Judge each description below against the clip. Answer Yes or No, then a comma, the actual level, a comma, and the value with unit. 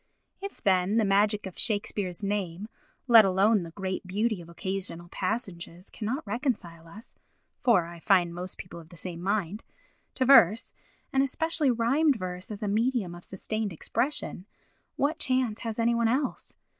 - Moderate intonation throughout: Yes, average, 4.5 semitones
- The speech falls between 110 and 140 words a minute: No, average, 160 wpm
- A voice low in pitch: No, high, 205 Hz